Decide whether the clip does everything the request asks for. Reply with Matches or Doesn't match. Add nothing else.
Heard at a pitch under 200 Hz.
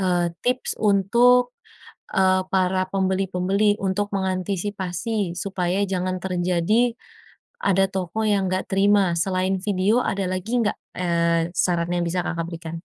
Matches